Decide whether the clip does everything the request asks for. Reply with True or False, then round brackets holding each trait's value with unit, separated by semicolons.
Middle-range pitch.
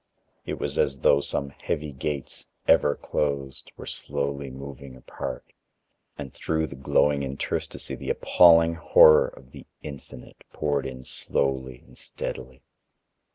False (70 Hz)